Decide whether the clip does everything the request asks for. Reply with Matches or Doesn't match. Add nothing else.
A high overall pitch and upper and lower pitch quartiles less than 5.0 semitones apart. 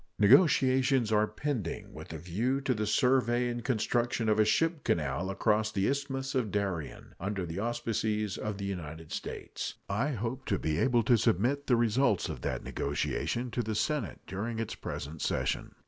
Doesn't match